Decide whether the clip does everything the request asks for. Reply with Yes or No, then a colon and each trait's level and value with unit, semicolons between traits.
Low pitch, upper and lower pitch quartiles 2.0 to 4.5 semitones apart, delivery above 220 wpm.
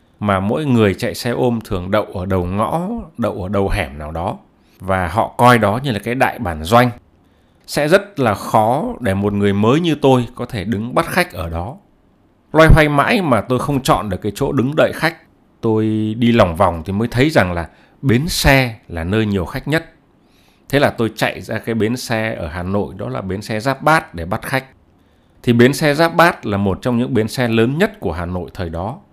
No: low, 110 Hz; wide, 5.4 semitones; average, 230 wpm